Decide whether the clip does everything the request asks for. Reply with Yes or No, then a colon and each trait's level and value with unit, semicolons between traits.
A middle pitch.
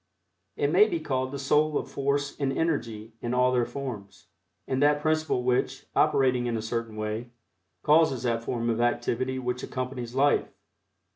No: low, 125 Hz